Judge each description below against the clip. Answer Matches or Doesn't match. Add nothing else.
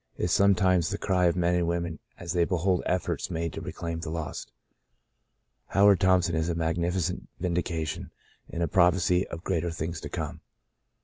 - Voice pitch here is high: Doesn't match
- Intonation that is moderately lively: Doesn't match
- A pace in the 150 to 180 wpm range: Matches